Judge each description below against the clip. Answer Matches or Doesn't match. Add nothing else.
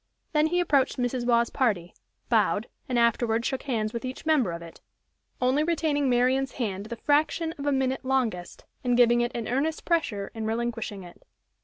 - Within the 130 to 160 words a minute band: Doesn't match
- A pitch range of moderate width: Matches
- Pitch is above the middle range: Matches